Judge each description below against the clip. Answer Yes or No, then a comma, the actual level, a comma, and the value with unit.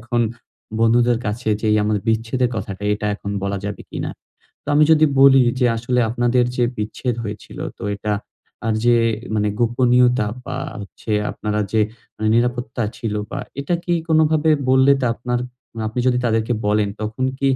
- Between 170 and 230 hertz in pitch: No, low, 120 Hz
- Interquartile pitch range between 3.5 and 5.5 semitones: No, average, 2.8 semitones